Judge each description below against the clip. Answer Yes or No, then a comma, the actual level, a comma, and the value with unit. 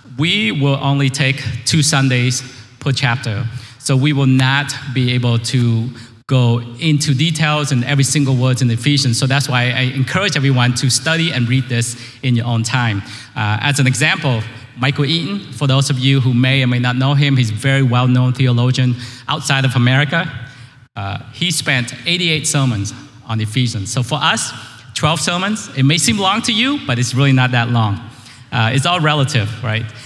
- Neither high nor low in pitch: No, low, 130 Hz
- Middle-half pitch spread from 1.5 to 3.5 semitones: Yes, average, 2.8 semitones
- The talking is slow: No, average, 195 wpm